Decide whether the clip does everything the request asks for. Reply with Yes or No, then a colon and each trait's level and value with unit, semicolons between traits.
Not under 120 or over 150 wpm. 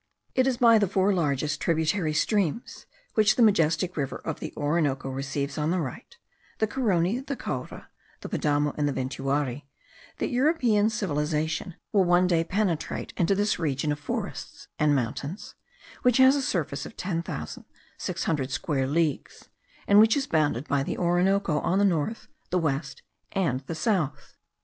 No: average, 165 wpm